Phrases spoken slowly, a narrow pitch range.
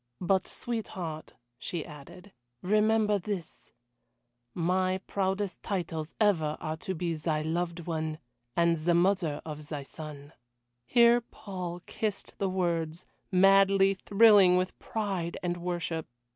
No: slow, 120 wpm; average, 3.3 semitones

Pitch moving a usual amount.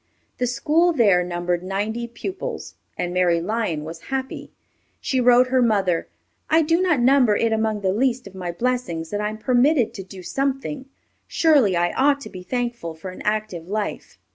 No: wide, 6.0 semitones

